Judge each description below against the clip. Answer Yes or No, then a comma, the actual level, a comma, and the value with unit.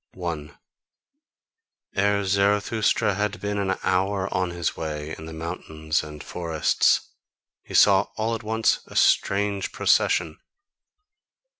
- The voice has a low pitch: Yes, very low, 95 Hz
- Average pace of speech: No, slow, 120 wpm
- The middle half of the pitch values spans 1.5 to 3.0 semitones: No, average, 4.0 semitones